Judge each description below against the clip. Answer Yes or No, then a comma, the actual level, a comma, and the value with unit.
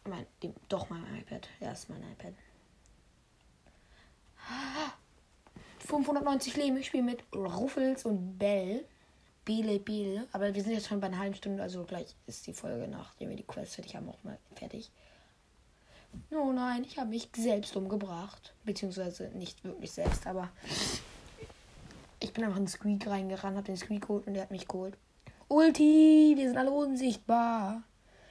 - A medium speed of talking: Yes, average, 160 wpm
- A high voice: Yes, high, 210 Hz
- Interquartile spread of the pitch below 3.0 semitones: No, average, 4.7 semitones